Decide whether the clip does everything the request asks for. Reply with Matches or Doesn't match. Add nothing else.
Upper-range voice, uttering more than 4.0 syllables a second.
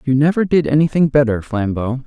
Doesn't match